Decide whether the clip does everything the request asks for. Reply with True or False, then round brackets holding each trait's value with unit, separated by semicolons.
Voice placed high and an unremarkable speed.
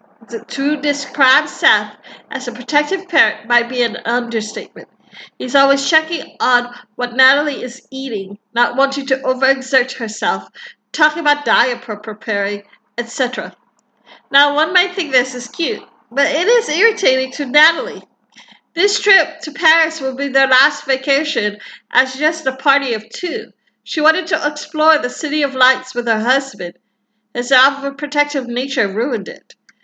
True (265 Hz; 150 wpm)